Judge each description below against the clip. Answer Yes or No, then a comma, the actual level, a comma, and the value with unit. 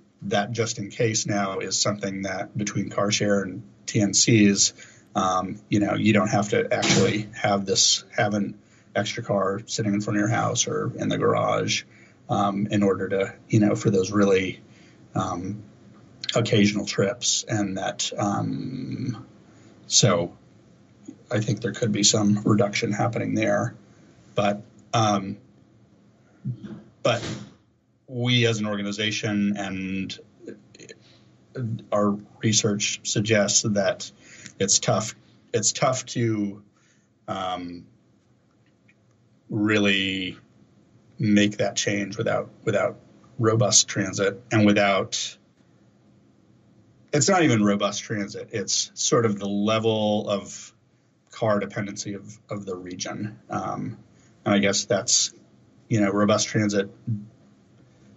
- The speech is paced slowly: Yes, slow, 120 wpm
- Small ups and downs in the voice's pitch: Yes, narrow, 1.5 semitones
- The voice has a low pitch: Yes, low, 105 Hz